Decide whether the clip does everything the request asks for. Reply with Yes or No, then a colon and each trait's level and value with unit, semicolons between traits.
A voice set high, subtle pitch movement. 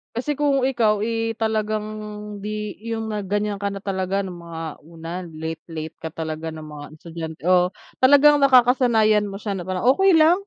No: high, 205 Hz; average, 5.3 semitones